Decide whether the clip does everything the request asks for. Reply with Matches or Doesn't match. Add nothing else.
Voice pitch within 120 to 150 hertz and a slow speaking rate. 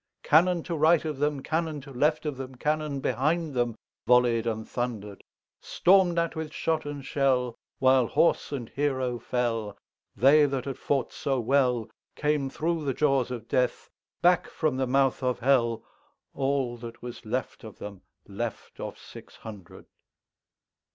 Matches